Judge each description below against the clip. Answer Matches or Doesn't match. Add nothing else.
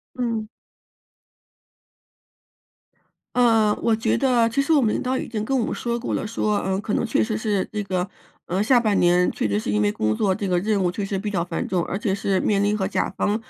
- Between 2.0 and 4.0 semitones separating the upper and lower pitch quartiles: Matches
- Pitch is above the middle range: Matches